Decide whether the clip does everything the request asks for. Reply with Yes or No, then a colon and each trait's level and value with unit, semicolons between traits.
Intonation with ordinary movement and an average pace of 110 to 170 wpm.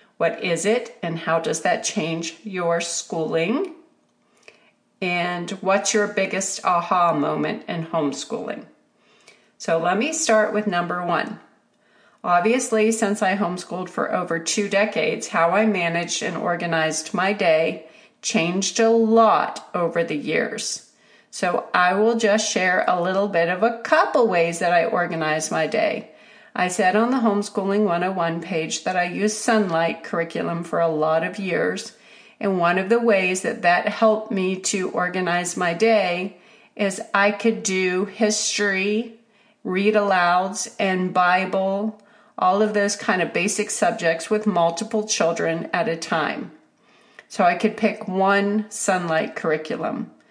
Yes: average, 3.9 semitones; average, 145 wpm